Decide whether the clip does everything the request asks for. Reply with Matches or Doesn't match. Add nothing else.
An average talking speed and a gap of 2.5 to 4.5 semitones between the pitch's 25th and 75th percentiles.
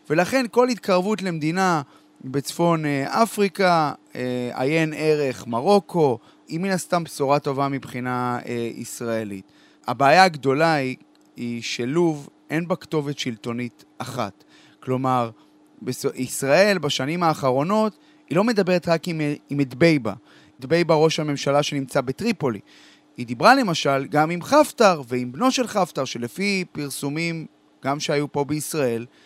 Doesn't match